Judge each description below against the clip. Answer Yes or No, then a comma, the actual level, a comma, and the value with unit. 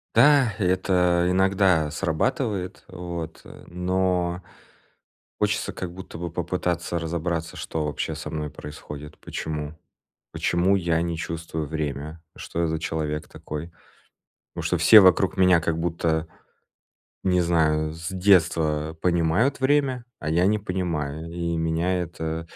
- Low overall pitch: Yes, very low, 85 Hz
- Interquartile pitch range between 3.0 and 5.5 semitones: No, narrow, 2.4 semitones